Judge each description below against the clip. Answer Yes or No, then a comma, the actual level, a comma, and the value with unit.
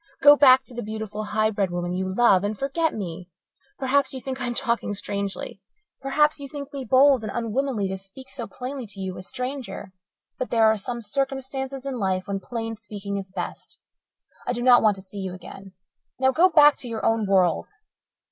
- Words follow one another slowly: No, fast, 205 wpm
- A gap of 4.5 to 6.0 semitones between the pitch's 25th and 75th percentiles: Yes, average, 5.1 semitones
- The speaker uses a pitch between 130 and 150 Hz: No, high, 225 Hz